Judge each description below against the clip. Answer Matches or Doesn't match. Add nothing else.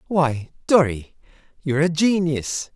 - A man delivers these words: Matches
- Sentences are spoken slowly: Matches